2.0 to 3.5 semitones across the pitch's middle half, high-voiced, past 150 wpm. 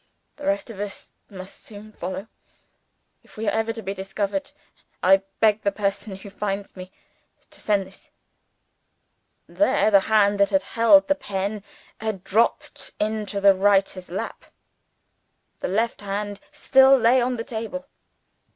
No: narrow, 2.6 semitones; high, 205 Hz; average, 140 wpm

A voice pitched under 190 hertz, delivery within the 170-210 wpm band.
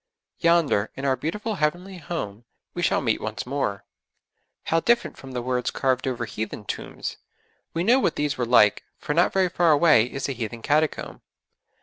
Yes: medium, 140 Hz; average, 180 wpm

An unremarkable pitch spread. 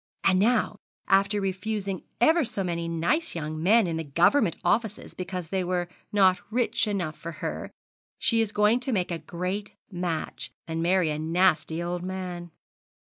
Yes: average, 3.5 semitones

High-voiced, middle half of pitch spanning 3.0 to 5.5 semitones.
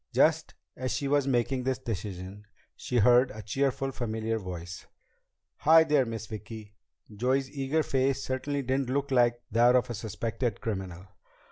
No: low, 120 Hz; average, 3.7 semitones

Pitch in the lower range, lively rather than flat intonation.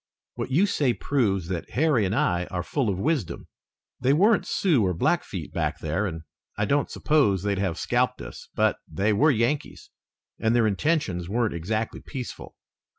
Yes: low, 110 Hz; wide, 6.9 semitones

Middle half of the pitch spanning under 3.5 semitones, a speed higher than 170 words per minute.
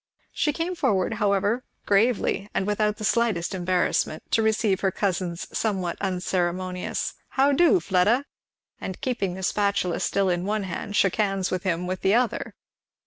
No: average, 3.1 semitones; average, 155 wpm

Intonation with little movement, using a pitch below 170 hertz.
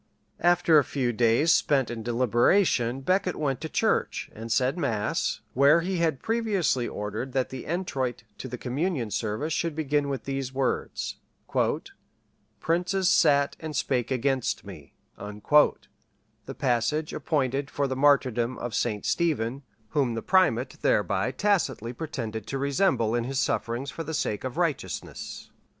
No: average, 4.8 semitones; low, 135 Hz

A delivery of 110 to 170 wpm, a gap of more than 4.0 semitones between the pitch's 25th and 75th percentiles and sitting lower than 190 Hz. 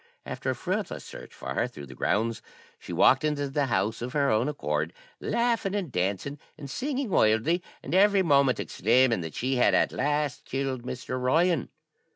No: average, 180 wpm; average, 5.2 semitones; low, 135 Hz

